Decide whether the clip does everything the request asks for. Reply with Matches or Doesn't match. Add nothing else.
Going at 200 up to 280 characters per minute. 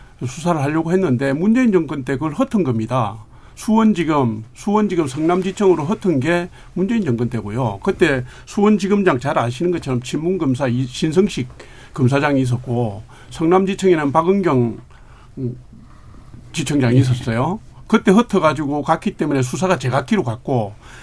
Doesn't match